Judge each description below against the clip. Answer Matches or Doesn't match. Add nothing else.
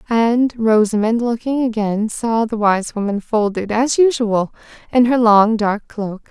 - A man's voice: Doesn't match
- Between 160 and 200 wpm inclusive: Doesn't match